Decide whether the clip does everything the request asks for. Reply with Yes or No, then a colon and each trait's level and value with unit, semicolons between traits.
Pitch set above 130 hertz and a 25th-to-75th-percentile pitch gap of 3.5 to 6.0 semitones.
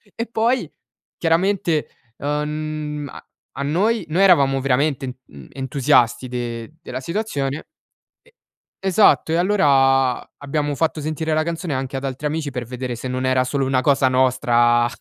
Yes: medium, 140 Hz; average, 3.8 semitones